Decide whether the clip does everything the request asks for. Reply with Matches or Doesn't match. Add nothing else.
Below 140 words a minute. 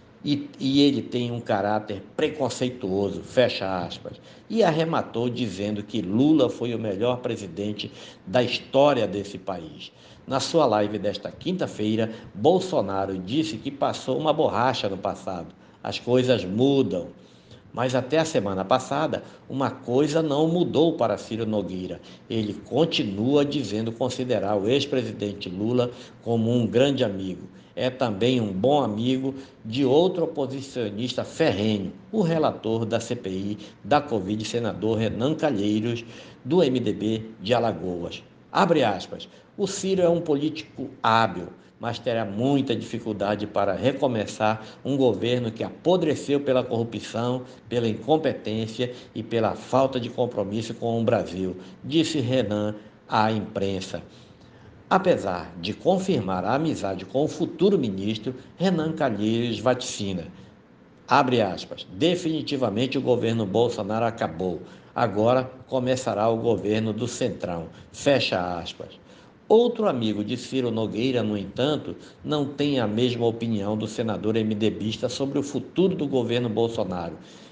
Matches